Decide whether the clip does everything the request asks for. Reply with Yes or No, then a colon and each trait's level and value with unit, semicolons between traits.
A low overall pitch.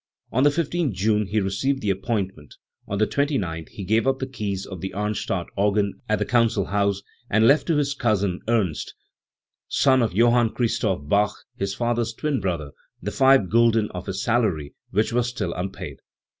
Yes: low, 105 Hz